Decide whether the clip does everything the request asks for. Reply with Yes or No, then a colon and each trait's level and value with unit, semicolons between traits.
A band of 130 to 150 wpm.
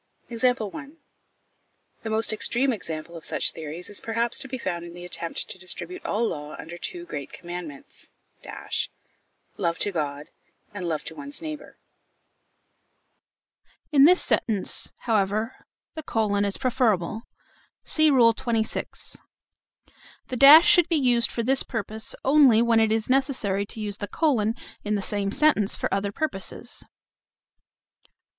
Yes: average, 140 wpm